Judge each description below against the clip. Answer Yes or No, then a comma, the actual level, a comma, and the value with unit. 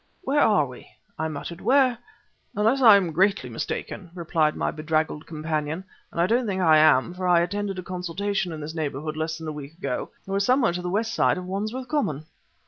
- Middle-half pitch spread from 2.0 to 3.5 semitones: No, average, 4.5 semitones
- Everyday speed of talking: No, fast, 210 wpm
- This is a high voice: No, medium, 175 Hz